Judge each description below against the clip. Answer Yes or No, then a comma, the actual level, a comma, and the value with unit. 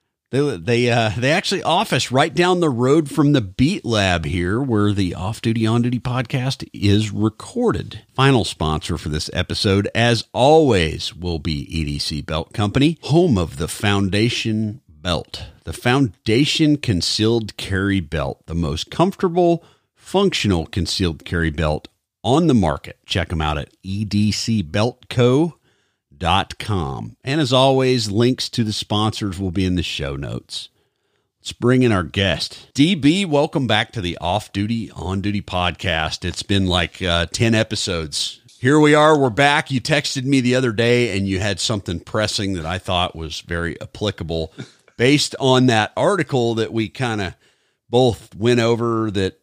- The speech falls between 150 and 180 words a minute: Yes, average, 155 wpm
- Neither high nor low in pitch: No, low, 110 Hz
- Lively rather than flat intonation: Yes, wide, 5.9 semitones